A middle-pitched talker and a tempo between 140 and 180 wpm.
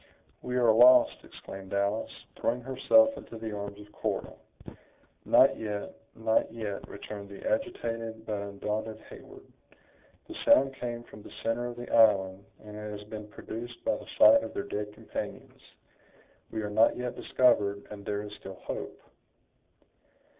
No: low, 110 Hz; average, 155 wpm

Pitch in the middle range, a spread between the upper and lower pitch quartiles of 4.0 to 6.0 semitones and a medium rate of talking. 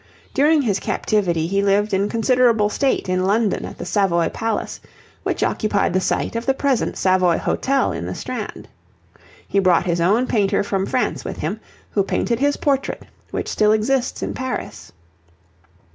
No: high, 210 Hz; average, 4.7 semitones; average, 165 wpm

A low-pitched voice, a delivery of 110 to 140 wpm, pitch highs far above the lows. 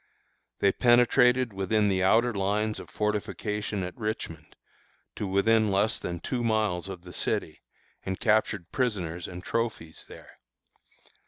No: low, 105 Hz; slow, 135 wpm; average, 3.0 semitones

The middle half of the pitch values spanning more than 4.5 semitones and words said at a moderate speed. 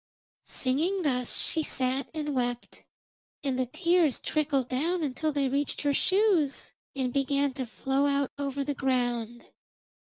No: average, 2.8 semitones; average, 145 wpm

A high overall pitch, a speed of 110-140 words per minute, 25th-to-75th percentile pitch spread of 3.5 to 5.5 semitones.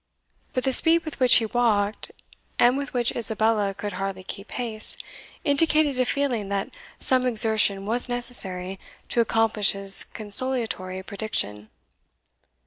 Yes: high, 220 Hz; slow, 135 wpm; average, 4.1 semitones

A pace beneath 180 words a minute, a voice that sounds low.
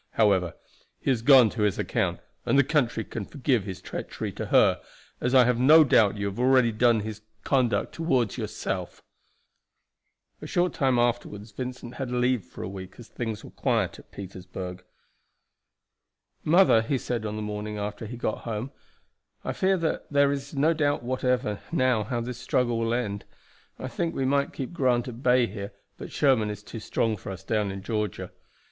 No: average, 185 wpm; low, 120 Hz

